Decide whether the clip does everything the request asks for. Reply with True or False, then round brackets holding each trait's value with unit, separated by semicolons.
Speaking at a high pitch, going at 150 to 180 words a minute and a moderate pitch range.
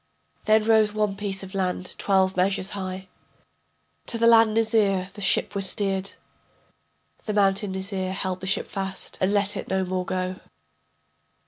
False (195 Hz; 155 wpm; 1.7 semitones)